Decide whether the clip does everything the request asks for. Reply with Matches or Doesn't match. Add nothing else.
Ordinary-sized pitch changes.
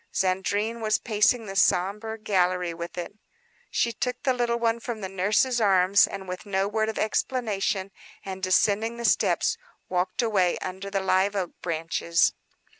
Matches